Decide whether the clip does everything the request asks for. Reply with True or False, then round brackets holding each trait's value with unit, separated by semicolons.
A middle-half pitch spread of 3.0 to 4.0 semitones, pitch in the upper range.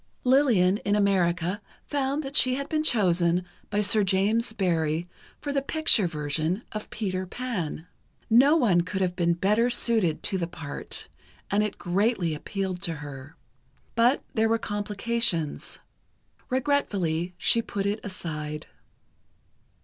False (5.2 semitones; 200 Hz)